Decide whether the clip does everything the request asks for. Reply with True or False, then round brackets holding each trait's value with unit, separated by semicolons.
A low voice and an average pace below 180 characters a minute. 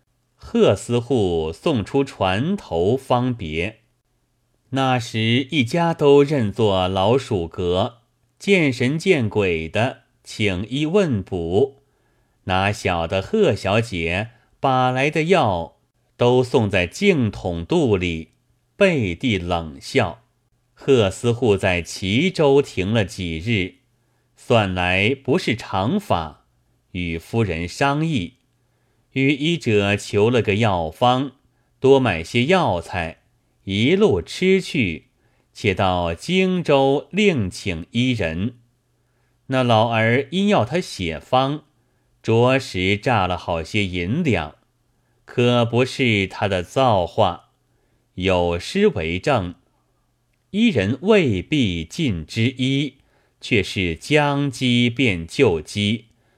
True (120 Hz; 145 characters per minute)